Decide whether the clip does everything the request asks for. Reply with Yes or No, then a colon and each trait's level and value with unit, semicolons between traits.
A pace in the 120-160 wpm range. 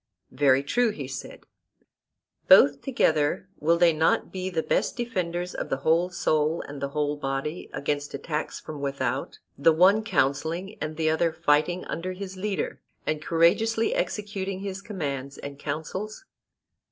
Yes: average, 150 wpm